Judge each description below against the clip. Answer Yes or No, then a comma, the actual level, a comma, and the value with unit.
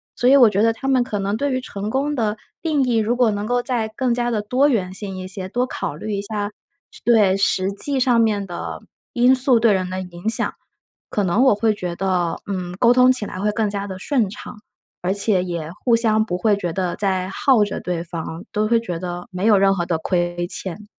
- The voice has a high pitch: Yes, high, 205 Hz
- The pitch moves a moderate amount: Yes, average, 4.2 semitones